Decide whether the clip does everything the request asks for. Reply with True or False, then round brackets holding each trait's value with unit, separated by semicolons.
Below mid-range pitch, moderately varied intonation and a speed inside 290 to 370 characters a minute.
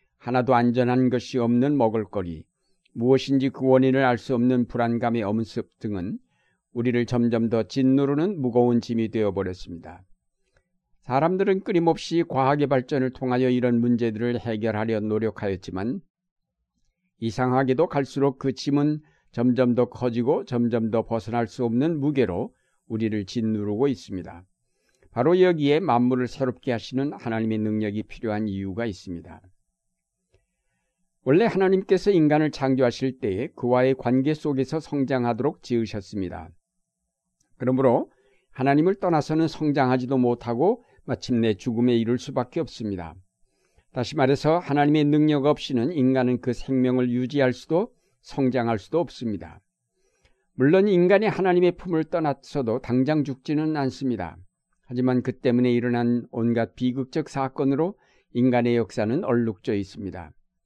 True (125 Hz; 3.8 semitones; 315 characters per minute)